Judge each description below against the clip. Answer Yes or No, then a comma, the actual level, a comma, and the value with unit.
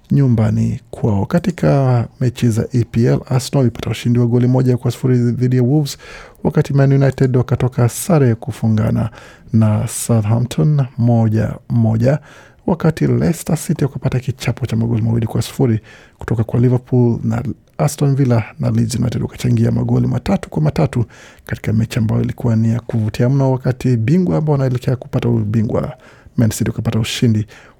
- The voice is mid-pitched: No, low, 120 Hz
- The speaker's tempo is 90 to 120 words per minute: No, average, 135 wpm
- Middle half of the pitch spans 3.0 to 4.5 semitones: No, narrow, 2.6 semitones